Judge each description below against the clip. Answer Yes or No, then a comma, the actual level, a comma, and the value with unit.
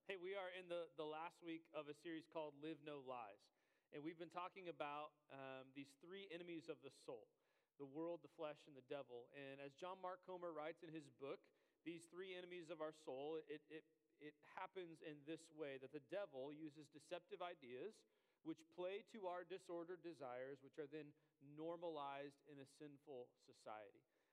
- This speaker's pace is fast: No, average, 185 wpm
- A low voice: No, medium, 160 Hz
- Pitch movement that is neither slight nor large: Yes, average, 3.3 semitones